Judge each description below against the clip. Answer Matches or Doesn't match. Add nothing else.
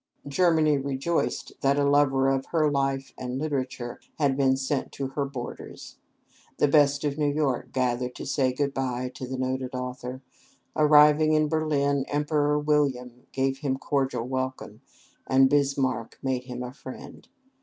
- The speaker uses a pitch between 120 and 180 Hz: Matches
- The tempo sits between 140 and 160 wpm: Matches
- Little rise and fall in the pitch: Matches